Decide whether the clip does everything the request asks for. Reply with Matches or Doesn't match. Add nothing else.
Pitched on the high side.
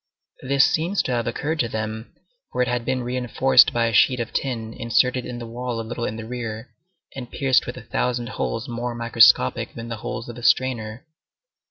Doesn't match